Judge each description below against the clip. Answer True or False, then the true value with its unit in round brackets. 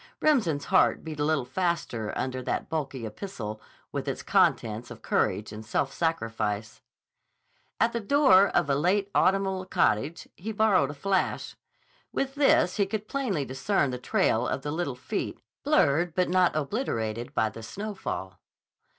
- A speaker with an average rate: True (155 wpm)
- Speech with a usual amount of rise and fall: False (8.7 semitones)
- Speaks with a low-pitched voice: False (155 Hz)